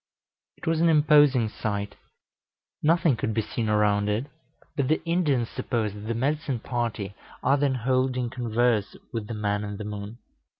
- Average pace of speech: Yes, average, 165 wpm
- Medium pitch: No, low, 120 Hz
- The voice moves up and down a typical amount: Yes, average, 4.6 semitones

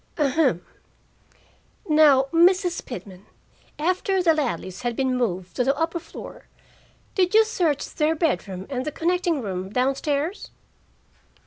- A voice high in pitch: Yes, very high, 295 Hz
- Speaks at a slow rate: Yes, slow, 130 wpm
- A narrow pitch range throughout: No, wide, 5.6 semitones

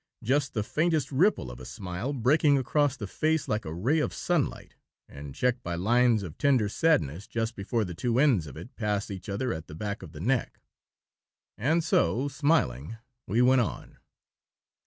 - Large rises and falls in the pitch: Yes, wide, 7.0 semitones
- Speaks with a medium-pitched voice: No, low, 115 Hz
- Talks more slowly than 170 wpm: No, average, 180 wpm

